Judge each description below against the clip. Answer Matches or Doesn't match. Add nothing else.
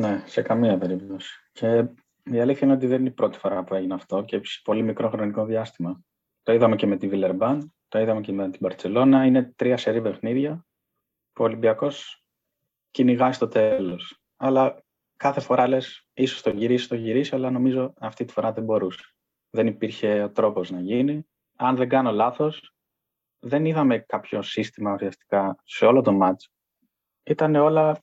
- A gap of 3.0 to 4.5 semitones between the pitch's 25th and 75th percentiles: Matches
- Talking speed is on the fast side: Matches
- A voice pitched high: Doesn't match